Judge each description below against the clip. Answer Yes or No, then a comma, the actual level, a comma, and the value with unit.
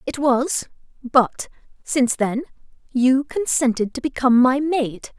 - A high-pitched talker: Yes, very high, 260 Hz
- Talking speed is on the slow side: Yes, slow, 125 wpm